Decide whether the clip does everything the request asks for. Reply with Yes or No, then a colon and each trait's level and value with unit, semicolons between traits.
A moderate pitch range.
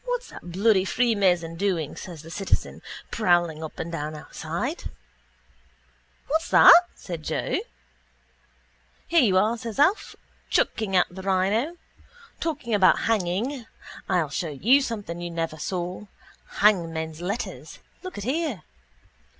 No: wide, 5.7 semitones